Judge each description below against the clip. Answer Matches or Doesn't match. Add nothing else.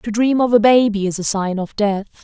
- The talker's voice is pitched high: Matches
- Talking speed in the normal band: Doesn't match